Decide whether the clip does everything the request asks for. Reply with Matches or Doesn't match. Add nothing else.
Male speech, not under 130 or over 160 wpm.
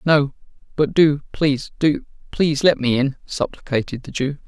Matches